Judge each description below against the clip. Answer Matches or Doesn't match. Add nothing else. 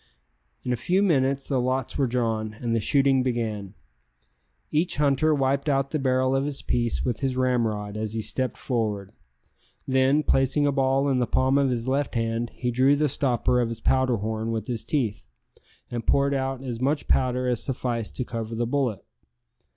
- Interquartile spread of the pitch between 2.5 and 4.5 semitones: Matches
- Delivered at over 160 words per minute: Matches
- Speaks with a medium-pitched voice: Doesn't match